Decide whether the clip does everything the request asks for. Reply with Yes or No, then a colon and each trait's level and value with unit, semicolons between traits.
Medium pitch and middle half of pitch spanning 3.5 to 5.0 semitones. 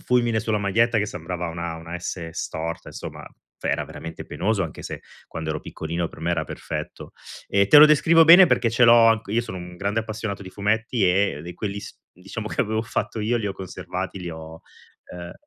No: low, 100 Hz; average, 4.5 semitones